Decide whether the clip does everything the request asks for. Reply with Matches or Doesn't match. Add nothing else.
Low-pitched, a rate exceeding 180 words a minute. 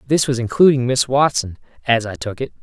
Matches